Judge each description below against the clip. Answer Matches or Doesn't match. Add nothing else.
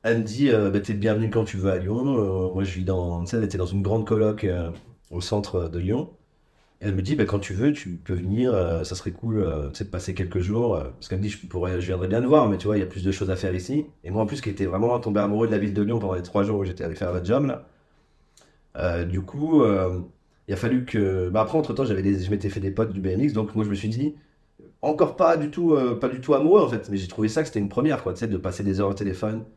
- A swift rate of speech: Matches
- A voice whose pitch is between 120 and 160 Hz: Doesn't match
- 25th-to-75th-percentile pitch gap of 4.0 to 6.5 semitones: Doesn't match